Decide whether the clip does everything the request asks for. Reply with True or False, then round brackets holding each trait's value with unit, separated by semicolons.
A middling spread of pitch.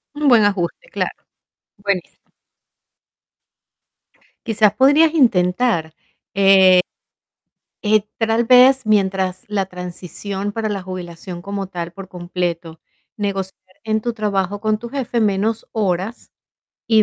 True (3.4 semitones)